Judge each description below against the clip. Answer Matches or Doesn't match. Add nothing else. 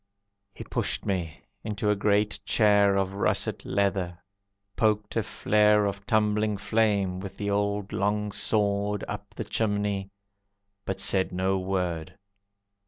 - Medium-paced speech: Doesn't match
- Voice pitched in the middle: Doesn't match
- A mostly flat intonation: Matches